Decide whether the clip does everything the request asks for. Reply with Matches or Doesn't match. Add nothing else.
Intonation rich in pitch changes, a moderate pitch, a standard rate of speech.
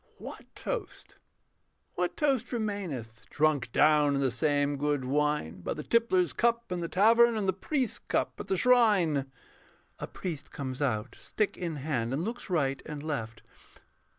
Matches